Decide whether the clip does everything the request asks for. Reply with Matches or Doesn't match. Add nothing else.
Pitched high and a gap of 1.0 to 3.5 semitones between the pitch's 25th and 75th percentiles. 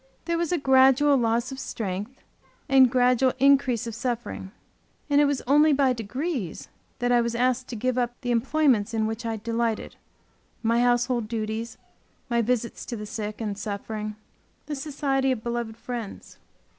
Matches